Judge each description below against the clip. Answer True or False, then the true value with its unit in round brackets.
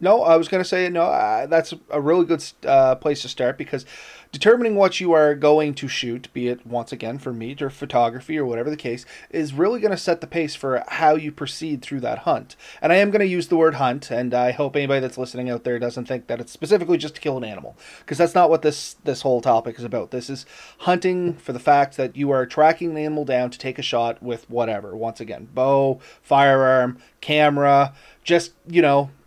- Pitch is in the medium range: True (145 Hz)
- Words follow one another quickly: True (230 wpm)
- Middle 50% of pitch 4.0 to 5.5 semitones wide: True (4.5 semitones)